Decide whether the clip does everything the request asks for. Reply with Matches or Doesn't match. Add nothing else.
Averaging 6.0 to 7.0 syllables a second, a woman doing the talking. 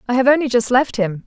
Matches